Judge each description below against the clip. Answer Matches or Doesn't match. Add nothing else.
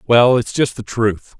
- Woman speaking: Doesn't match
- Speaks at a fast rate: Matches